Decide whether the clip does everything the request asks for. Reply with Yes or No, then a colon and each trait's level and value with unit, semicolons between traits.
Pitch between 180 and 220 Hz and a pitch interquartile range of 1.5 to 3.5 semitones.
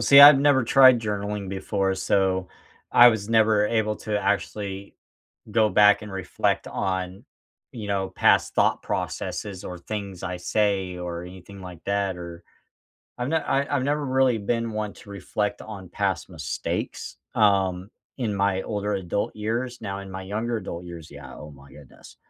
No: low, 100 Hz; average, 2.8 semitones